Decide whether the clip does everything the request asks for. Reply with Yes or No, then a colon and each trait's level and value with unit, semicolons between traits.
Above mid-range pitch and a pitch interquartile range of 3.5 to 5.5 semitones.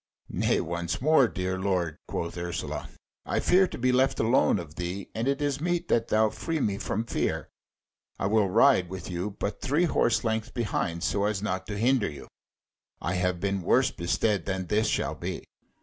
No: low, 105 Hz; average, 4.9 semitones